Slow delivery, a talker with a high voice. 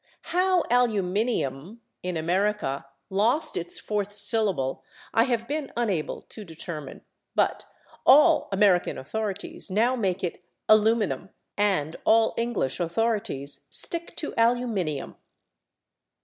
Yes: slow, 105 wpm; high, 205 Hz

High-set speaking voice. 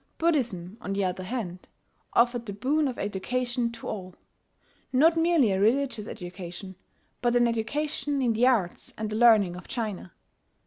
Yes: high, 230 Hz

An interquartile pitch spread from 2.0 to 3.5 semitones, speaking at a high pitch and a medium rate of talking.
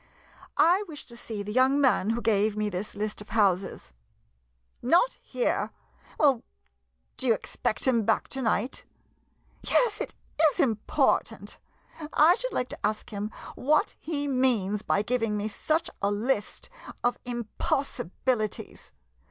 No: average, 4.5 semitones; high, 235 Hz; average, 145 wpm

